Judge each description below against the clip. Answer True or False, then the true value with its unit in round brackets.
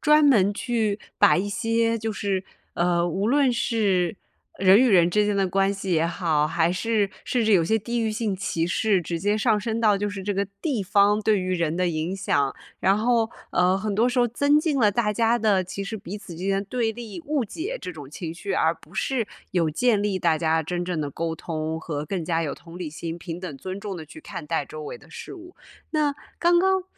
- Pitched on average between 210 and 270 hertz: False (200 Hz)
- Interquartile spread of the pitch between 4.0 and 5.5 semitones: True (4.7 semitones)